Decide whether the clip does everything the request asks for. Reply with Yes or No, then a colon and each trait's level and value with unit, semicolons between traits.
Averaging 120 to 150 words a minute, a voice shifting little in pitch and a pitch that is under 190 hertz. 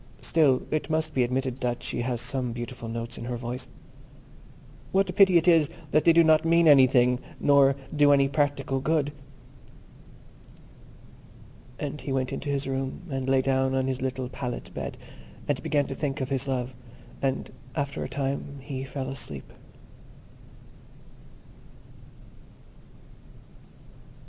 Yes: average, 145 wpm; narrow, 2.1 semitones; low, 135 Hz